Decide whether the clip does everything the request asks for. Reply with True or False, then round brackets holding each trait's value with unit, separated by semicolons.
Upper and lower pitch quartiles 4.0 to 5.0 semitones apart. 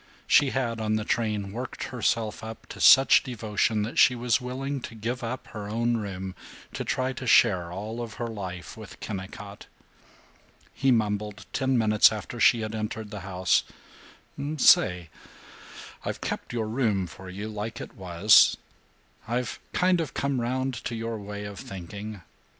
False (2.9 semitones)